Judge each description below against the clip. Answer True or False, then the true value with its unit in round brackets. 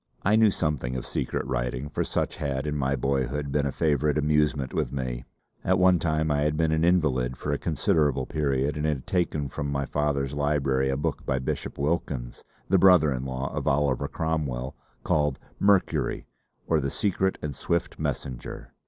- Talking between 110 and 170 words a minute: False (180 wpm)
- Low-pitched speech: True (75 Hz)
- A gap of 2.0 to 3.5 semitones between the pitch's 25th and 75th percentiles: True (2.7 semitones)